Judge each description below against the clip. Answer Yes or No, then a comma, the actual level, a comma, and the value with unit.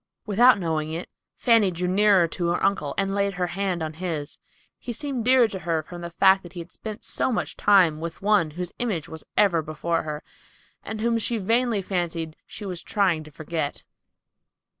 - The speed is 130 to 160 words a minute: No, average, 195 wpm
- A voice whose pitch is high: No, medium, 180 Hz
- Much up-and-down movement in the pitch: No, average, 4.0 semitones